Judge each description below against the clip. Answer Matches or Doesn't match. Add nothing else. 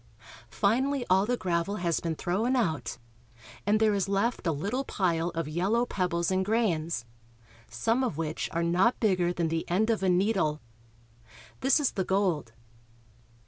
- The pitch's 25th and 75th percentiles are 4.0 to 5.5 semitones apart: Matches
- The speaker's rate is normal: Matches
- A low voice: Doesn't match